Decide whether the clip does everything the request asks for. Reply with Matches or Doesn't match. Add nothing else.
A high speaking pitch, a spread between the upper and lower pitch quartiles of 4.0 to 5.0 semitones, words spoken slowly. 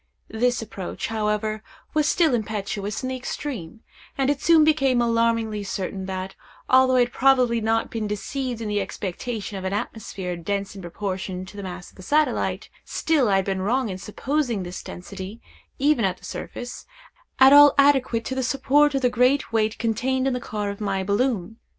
Doesn't match